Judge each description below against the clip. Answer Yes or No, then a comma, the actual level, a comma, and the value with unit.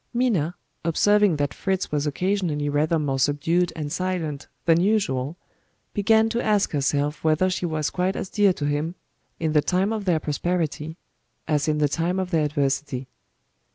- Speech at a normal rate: Yes, average, 165 wpm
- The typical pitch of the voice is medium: Yes, medium, 160 Hz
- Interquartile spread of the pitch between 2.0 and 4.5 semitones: Yes, average, 4.1 semitones